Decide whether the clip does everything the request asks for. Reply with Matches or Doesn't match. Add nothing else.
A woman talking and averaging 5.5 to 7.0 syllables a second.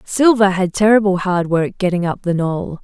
Doesn't match